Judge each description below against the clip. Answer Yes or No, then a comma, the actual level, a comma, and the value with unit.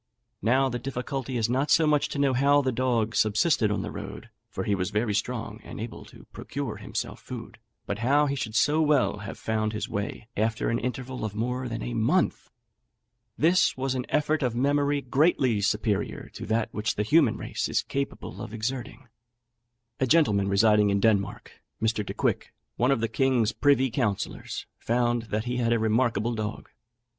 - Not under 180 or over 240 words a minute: Yes, average, 185 wpm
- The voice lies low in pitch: Yes, low, 120 Hz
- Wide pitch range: No, average, 3.7 semitones